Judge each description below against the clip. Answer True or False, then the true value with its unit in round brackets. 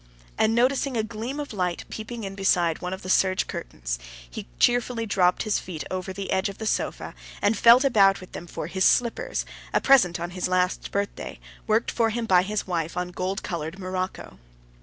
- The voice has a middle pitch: False (195 Hz)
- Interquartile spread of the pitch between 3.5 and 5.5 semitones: True (3.9 semitones)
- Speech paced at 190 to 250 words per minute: True (200 wpm)